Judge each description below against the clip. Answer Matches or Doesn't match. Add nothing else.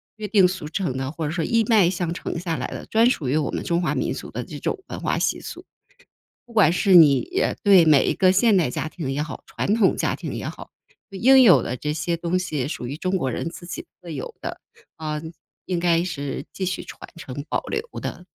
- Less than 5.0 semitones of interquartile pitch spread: Matches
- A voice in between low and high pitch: Matches